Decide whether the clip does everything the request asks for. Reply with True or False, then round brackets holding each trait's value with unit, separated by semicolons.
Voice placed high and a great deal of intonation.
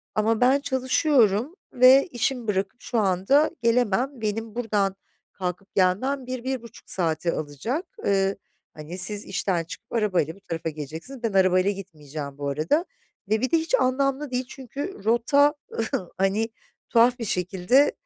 True (220 Hz; 5.7 semitones)